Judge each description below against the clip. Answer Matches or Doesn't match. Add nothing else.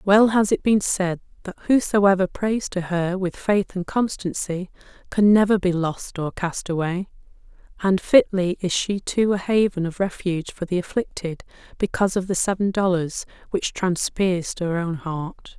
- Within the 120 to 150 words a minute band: Doesn't match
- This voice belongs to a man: Doesn't match